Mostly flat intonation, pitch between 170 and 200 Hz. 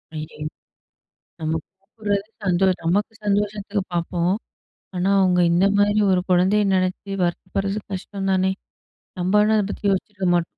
Yes: narrow, 2.1 semitones; high, 190 Hz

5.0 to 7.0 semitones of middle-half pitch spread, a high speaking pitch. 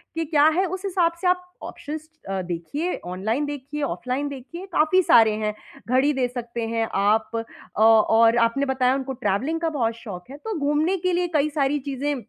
Yes: wide, 5.4 semitones; very high, 275 Hz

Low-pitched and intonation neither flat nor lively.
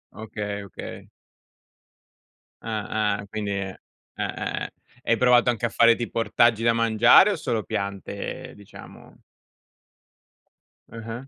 No: low, 110 Hz; narrow, 2.3 semitones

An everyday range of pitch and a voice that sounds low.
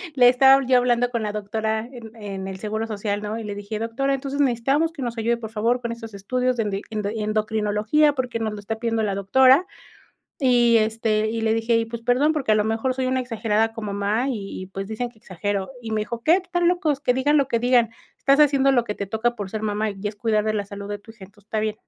No: average, 3.0 semitones; high, 225 Hz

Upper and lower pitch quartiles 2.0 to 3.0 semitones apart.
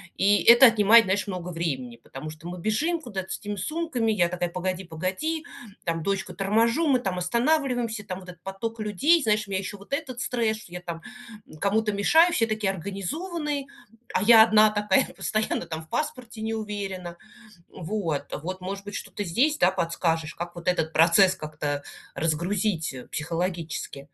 No: average, 4.6 semitones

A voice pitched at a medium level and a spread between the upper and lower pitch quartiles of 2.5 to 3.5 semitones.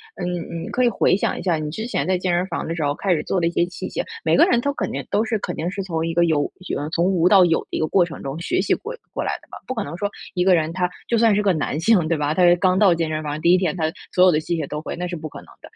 Yes: medium, 175 Hz; average, 2.9 semitones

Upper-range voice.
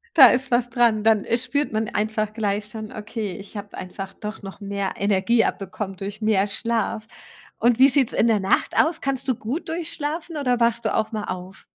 Yes: high, 220 Hz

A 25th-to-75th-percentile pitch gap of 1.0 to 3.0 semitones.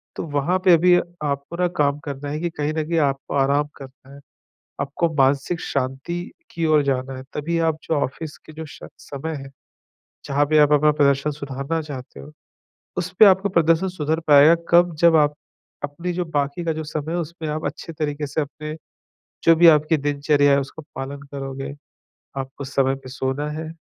Yes: narrow, 2.6 semitones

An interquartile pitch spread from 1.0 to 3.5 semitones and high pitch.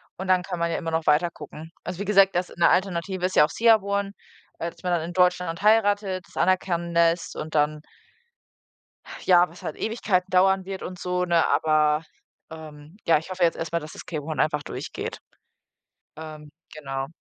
No: average, 2.9 semitones; medium, 175 Hz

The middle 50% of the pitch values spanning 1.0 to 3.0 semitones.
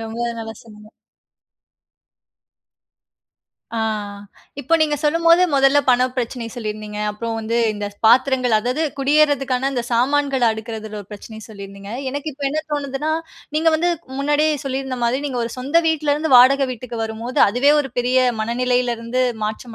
No: average, 4.0 semitones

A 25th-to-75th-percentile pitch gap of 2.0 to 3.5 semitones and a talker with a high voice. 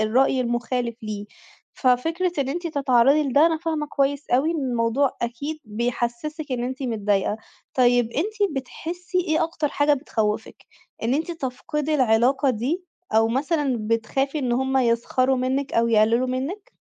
No: average, 4.3 semitones; very high, 265 Hz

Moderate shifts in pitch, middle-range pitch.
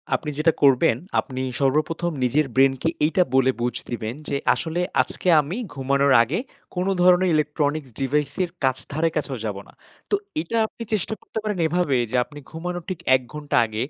Yes: average, 4.5 semitones; medium, 150 Hz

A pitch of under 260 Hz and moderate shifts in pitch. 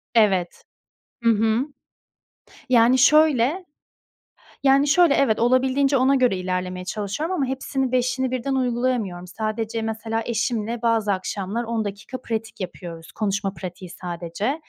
Yes: high, 230 Hz; average, 4.5 semitones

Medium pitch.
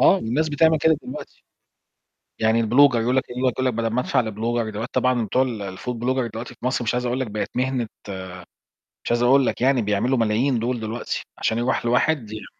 No: low, 120 Hz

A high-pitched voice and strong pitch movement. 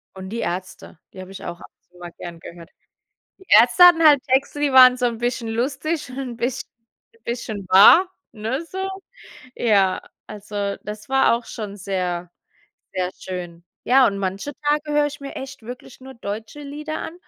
Yes: high, 235 Hz; wide, 6.4 semitones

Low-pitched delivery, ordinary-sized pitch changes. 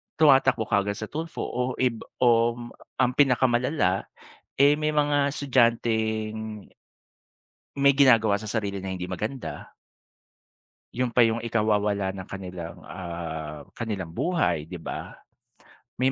Yes: low, 115 Hz; average, 4.7 semitones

